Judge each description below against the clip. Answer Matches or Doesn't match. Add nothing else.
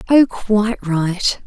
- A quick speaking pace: Doesn't match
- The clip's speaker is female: Matches